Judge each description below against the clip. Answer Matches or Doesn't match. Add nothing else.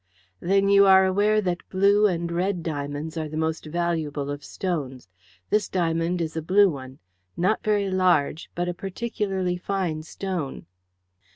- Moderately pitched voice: Matches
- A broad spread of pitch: Doesn't match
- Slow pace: Doesn't match